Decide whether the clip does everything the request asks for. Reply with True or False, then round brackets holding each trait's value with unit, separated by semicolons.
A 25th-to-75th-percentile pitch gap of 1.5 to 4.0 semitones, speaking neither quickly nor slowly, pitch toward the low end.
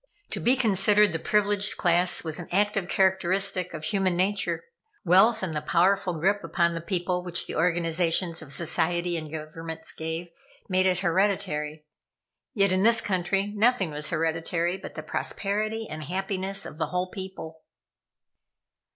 False (3.0 semitones; 150 wpm; 180 Hz)